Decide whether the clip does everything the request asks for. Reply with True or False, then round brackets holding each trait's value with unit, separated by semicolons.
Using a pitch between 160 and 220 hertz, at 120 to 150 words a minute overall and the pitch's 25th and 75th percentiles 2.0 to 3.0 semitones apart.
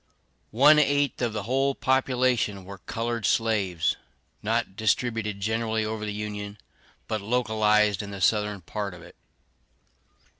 False (110 Hz; 135 wpm; 2.7 semitones)